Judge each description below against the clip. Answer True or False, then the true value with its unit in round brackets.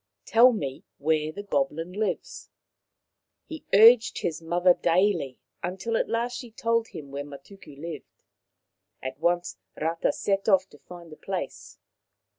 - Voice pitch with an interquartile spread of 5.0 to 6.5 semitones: True (5.6 semitones)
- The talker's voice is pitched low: False (175 Hz)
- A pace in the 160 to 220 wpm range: False (145 wpm)